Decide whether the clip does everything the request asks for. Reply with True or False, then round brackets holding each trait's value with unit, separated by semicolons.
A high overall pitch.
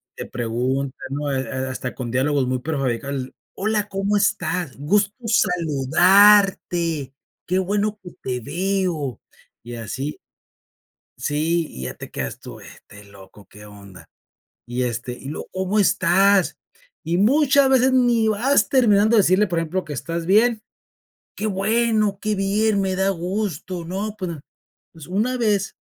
False (180 Hz)